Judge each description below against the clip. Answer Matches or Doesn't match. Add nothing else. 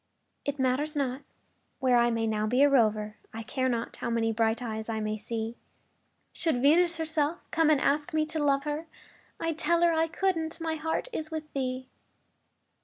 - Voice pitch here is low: Doesn't match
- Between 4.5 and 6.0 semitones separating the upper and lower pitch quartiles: Matches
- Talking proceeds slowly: Doesn't match